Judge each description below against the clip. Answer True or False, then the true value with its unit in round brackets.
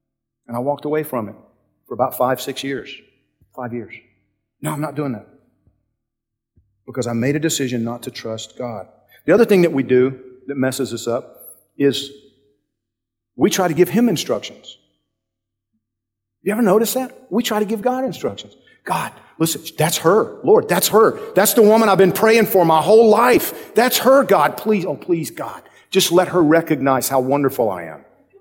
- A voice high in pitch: False (140 Hz)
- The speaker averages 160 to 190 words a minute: True (180 wpm)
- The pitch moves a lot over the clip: True (8.2 semitones)